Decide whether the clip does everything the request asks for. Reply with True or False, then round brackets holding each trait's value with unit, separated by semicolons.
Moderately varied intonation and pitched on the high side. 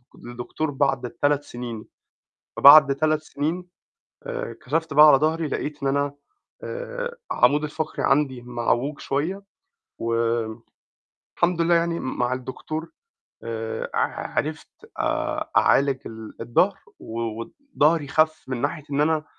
False (3.6 semitones; 145 Hz)